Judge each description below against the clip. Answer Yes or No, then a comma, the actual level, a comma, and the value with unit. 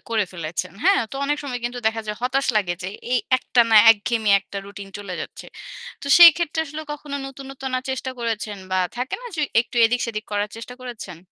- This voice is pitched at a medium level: No, high, 235 Hz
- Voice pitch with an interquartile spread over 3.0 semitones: Yes, average, 4.5 semitones